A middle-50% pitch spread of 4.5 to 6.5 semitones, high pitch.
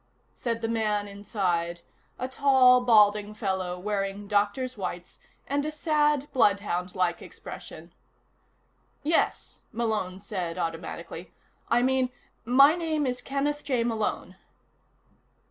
Yes: wide, 5.4 semitones; high, 220 Hz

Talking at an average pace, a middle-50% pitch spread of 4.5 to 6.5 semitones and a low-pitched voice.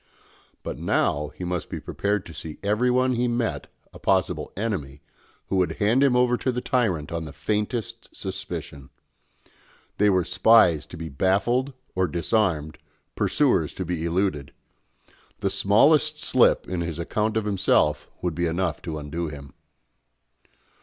Yes: average, 155 wpm; wide, 5.5 semitones; very low, 95 Hz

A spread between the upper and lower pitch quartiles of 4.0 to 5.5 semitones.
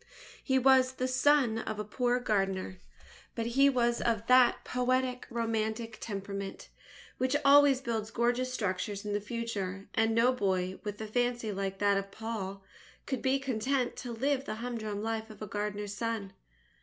No: average, 3.5 semitones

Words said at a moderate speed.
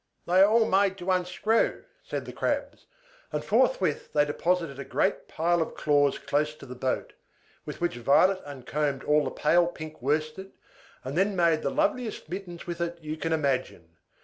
Yes: average, 175 wpm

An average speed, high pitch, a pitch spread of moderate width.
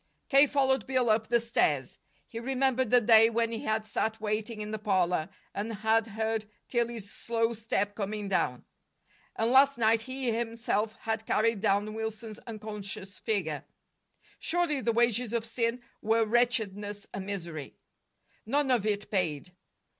No: average, 150 wpm; high, 220 Hz; narrow, 2.2 semitones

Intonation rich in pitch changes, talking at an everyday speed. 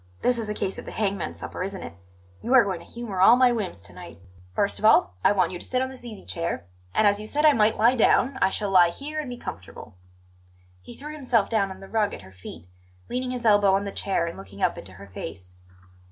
No: wide, 6.1 semitones; fast, 255 wpm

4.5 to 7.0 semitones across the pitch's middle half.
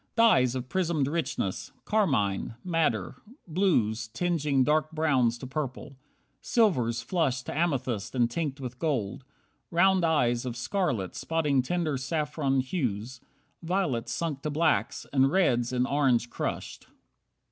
Yes: average, 5.0 semitones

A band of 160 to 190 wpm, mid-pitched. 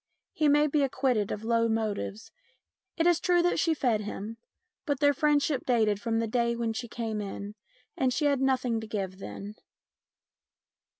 No: average, 175 wpm; high, 235 Hz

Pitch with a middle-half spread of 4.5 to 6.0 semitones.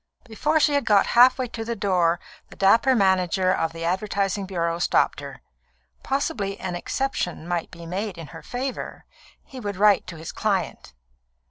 Yes: average, 5.1 semitones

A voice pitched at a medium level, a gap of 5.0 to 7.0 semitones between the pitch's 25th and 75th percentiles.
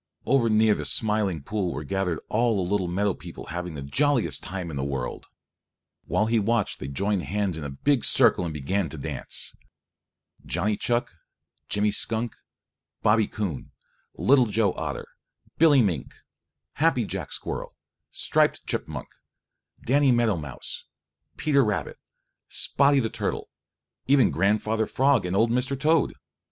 No: low, 105 Hz; average, 5.3 semitones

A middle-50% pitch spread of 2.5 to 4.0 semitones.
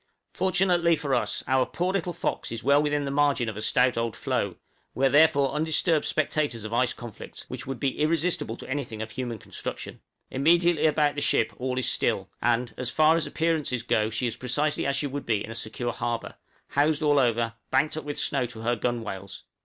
No: average, 4.4 semitones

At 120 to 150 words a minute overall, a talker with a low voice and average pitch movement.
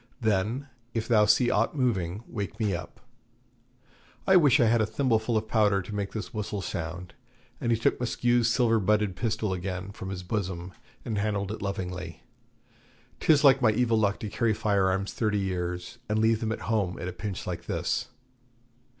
No: average, 185 wpm; low, 105 Hz; average, 3.1 semitones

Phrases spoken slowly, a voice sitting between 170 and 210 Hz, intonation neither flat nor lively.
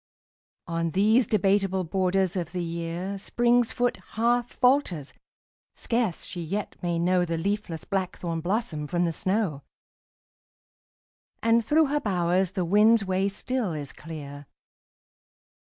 Yes: slow, 125 wpm; high, 190 Hz; average, 4.5 semitones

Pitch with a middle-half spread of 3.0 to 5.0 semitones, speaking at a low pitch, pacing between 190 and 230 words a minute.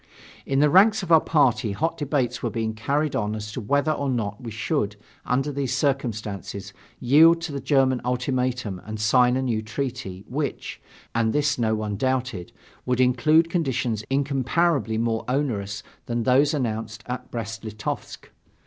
No: average, 4.3 semitones; low, 125 Hz; average, 160 wpm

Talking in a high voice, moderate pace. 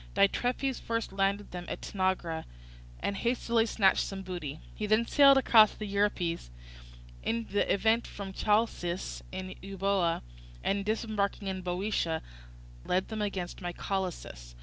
No: high, 195 Hz; slow, 130 wpm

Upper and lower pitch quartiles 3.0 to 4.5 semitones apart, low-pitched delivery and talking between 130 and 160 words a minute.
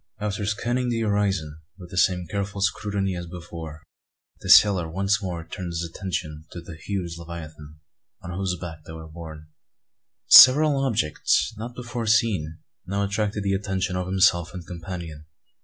Yes: average, 3.5 semitones; very low, 90 Hz; average, 155 wpm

